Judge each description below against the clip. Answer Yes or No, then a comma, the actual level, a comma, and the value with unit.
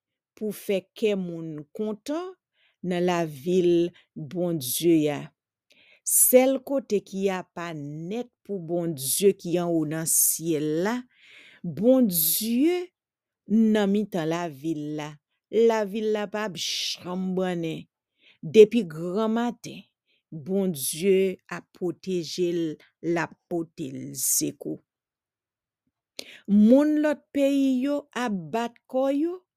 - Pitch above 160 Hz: Yes, medium, 185 Hz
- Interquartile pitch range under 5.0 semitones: No, average, 5.3 semitones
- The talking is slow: Yes, slow, 115 wpm